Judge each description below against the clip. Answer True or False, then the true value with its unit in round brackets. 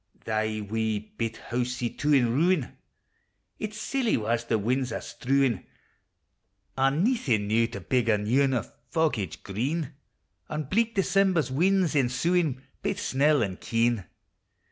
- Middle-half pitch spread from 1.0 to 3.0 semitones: False (5.6 semitones)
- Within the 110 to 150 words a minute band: True (140 wpm)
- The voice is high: False (130 Hz)